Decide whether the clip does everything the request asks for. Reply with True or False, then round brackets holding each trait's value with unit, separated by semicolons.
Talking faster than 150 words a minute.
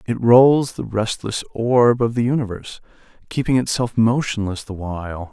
False (145 wpm)